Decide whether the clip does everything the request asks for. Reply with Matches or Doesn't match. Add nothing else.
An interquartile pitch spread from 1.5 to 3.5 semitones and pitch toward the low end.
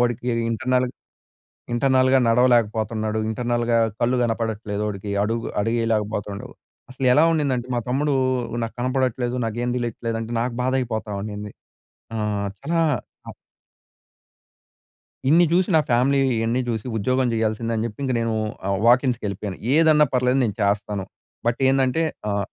Matches